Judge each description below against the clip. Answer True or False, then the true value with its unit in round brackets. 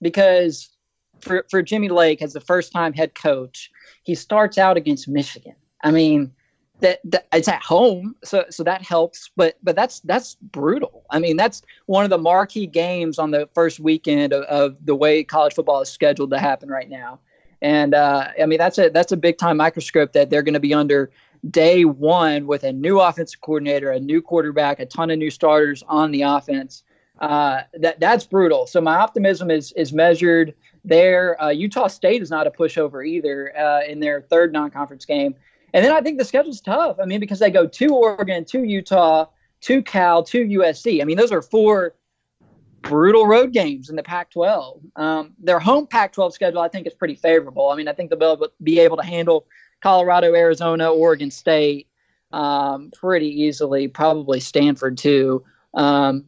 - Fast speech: False (190 wpm)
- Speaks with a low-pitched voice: False (165 Hz)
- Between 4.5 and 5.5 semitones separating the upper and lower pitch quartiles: False (3.9 semitones)